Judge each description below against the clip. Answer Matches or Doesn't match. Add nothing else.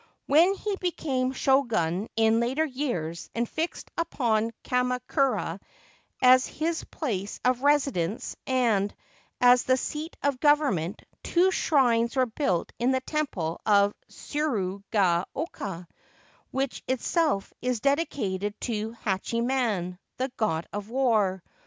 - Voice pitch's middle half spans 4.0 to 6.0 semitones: Matches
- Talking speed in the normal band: Doesn't match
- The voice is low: Doesn't match